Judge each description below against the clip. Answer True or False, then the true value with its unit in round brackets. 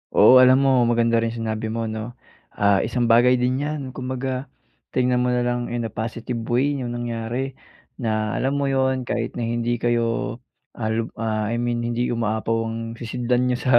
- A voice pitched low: True (120 Hz)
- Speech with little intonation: True (1.7 semitones)